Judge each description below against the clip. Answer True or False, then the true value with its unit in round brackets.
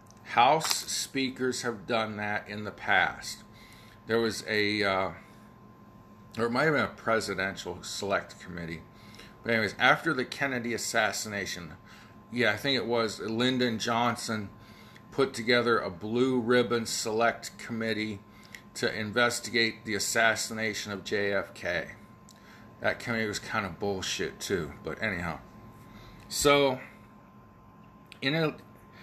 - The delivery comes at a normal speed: False (120 wpm)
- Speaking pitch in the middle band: False (110 Hz)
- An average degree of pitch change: False (2.3 semitones)